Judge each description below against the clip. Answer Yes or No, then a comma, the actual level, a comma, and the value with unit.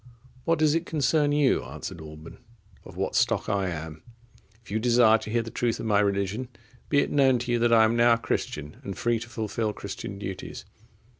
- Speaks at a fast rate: Yes, fast, 210 wpm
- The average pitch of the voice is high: No, low, 115 Hz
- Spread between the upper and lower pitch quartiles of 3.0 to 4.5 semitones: Yes, average, 3.7 semitones